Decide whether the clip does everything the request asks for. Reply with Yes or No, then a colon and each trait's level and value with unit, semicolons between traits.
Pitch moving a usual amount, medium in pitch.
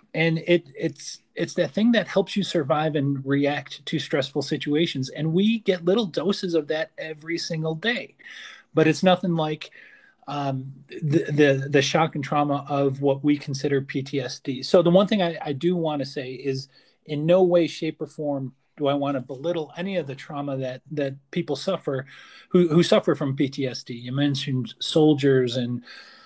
Yes: average, 3.9 semitones; medium, 155 Hz